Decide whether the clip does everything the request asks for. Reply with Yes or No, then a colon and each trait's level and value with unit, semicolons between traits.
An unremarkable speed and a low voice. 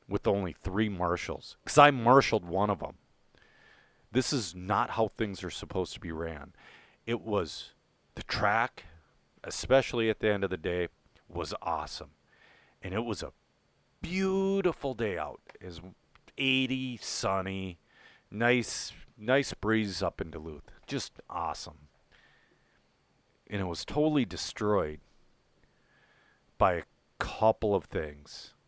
No: slow, 130 wpm; low, 105 Hz